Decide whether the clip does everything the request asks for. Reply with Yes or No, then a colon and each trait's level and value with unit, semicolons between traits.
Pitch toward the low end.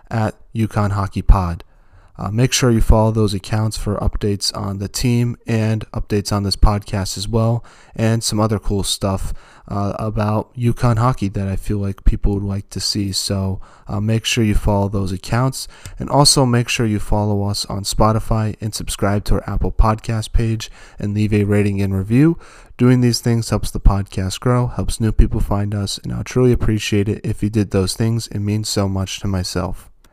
Yes: low, 105 Hz